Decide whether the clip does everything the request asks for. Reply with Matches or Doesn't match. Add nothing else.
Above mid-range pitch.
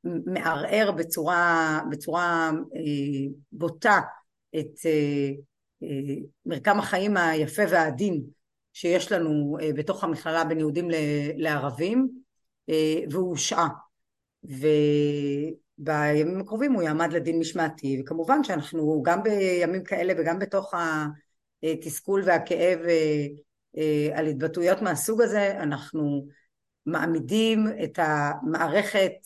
Doesn't match